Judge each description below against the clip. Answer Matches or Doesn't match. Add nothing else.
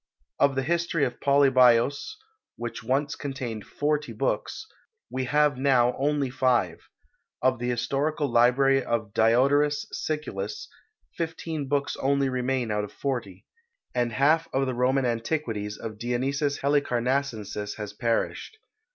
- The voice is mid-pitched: Doesn't match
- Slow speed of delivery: Matches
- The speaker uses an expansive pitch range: Doesn't match